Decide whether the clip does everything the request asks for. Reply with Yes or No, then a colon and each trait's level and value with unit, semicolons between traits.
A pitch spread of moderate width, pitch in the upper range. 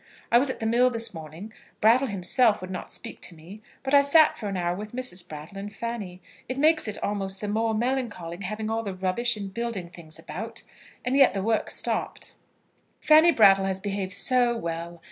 Yes: average, 4.4 semitones; high, 210 Hz